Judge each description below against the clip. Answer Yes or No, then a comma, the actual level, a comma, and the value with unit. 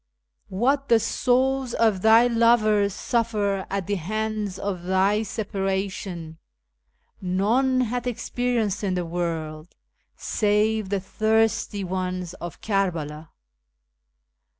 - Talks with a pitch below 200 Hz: No, high, 205 Hz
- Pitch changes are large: No, average, 3.4 semitones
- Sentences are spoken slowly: Yes, slow, 105 wpm